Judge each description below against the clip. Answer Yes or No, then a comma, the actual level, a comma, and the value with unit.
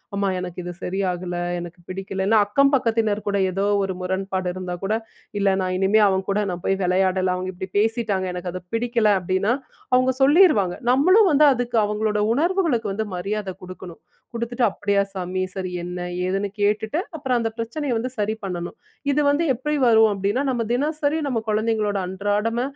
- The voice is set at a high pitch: Yes, high, 205 Hz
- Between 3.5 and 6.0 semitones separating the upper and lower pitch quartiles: Yes, average, 4.2 semitones